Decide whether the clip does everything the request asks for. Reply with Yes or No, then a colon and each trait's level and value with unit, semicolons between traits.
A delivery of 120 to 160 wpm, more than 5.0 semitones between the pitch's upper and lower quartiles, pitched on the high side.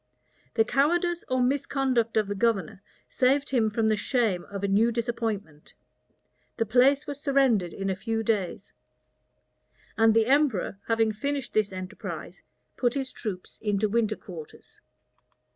No: average, 145 wpm; average, 4.2 semitones; high, 225 Hz